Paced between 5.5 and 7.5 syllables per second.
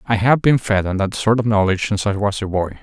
Yes: 6.3 syllables/s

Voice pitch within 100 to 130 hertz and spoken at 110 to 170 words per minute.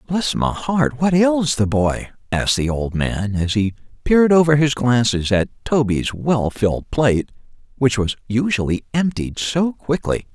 Yes: low, 125 Hz; average, 160 wpm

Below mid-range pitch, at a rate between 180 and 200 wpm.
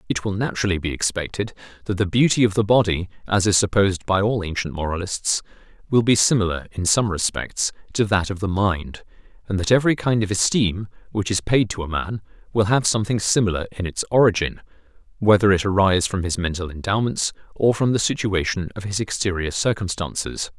Yes: low, 100 Hz; average, 185 wpm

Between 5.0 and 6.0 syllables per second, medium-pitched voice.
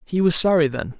Yes: 5.6 syllables/s; medium, 165 Hz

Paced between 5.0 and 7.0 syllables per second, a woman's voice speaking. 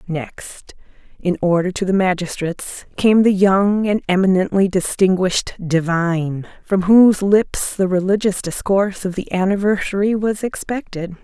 No: 4.6 syllables/s; female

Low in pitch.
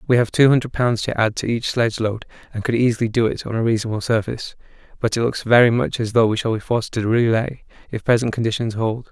Yes: low, 115 Hz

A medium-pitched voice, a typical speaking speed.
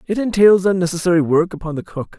Yes: medium, 180 Hz; average, 190 wpm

